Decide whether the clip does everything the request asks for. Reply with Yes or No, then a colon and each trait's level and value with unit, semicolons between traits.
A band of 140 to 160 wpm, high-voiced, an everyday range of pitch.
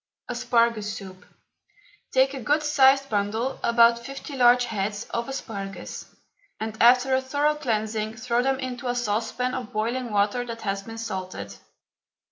Yes: average, 145 wpm; high, 235 Hz; average, 3.3 semitones